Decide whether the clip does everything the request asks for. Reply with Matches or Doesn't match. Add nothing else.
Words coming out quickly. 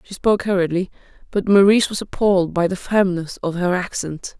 Doesn't match